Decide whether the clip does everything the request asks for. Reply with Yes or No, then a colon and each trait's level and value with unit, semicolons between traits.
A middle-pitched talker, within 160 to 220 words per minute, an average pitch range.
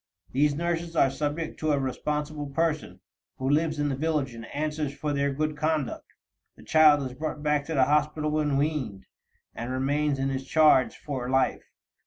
No: medium, 150 Hz; average, 180 wpm; narrow, 2.2 semitones